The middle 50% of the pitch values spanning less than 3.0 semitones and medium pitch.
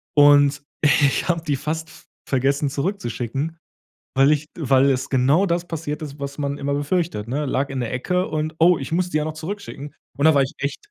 Yes: narrow, 2.6 semitones; medium, 145 Hz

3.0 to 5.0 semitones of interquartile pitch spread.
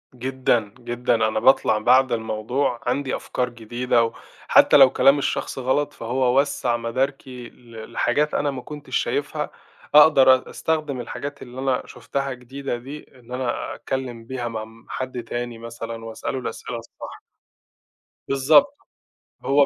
No: narrow, 2.5 semitones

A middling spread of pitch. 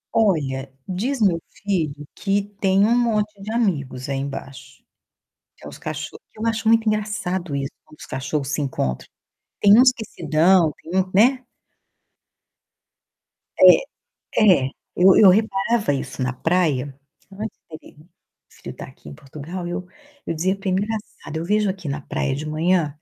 No: wide, 6.3 semitones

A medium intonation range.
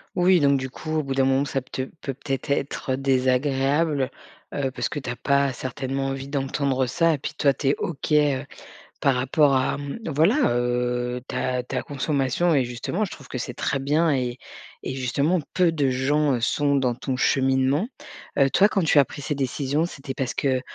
No: narrow, 2.1 semitones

